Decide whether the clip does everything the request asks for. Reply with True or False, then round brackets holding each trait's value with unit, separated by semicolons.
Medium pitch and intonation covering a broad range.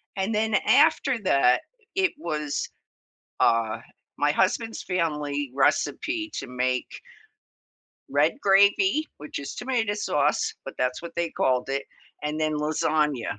True (155 Hz; 6.6 semitones)